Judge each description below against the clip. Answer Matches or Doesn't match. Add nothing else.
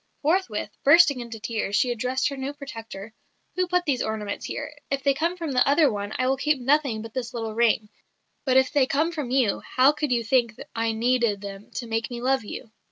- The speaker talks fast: Matches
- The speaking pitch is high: Matches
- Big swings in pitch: Doesn't match